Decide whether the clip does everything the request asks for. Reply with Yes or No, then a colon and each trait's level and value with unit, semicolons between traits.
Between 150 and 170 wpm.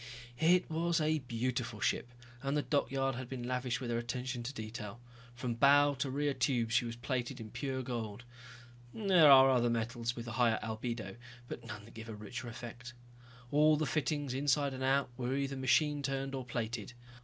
No: average, 190 wpm